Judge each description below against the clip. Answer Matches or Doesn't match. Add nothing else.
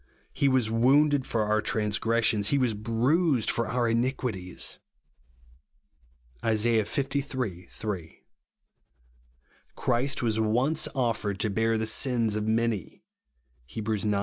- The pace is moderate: Doesn't match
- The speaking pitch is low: Matches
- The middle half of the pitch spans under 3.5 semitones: Matches